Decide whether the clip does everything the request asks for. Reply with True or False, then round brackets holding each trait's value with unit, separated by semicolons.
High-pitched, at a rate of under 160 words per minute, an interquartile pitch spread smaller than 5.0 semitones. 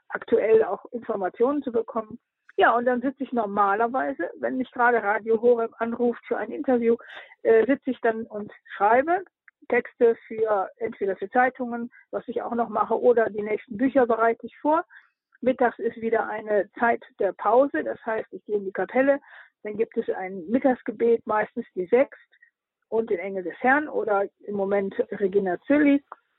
False (235 Hz; 170 wpm; 3.4 semitones)